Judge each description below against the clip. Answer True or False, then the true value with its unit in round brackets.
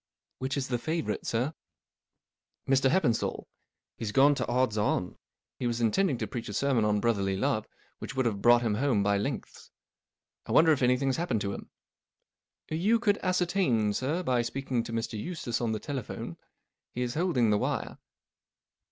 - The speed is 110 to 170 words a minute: False (185 wpm)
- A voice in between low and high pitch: False (125 Hz)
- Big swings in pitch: False (4.3 semitones)